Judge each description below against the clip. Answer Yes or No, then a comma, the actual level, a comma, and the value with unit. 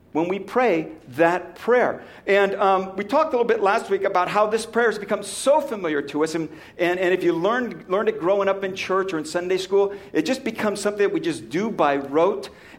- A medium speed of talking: No, fast, 235 wpm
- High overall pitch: Yes, high, 195 Hz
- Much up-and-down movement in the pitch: No, average, 3.4 semitones